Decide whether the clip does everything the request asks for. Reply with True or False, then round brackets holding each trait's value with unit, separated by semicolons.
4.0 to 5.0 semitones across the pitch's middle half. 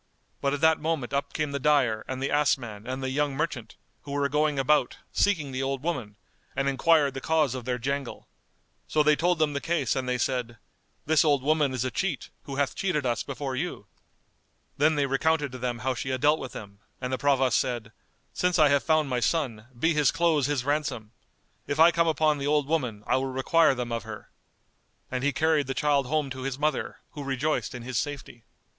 False (3.0 semitones)